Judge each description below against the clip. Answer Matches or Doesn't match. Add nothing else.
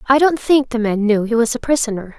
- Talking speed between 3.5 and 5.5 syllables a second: Doesn't match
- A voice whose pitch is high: Matches